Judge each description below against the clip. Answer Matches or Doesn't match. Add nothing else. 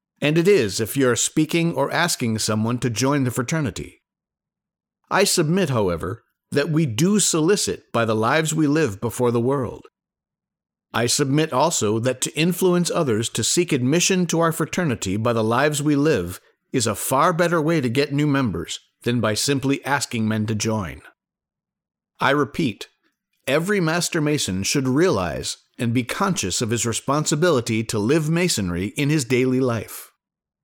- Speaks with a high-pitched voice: Doesn't match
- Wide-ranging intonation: Matches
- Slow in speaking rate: Doesn't match